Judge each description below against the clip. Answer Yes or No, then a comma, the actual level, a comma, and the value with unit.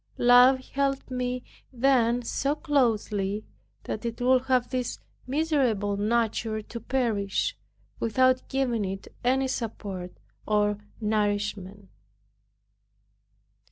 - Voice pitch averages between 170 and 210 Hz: No, high, 235 Hz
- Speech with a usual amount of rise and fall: Yes, average, 3.7 semitones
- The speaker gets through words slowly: Yes, slow, 95 wpm